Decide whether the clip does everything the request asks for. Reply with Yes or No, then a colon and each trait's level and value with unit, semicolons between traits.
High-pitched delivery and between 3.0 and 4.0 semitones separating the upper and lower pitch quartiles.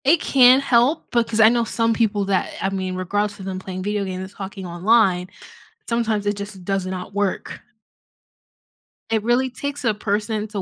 Yes: high, 205 Hz; average, 3.3 semitones